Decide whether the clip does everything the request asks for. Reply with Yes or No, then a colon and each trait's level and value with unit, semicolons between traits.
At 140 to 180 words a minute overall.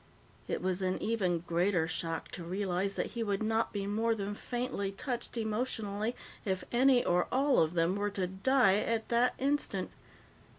Yes: average, 170 wpm